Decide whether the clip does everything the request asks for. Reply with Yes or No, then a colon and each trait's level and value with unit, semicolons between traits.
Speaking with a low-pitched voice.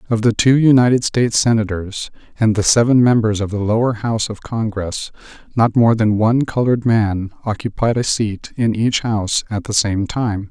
Yes: low, 110 Hz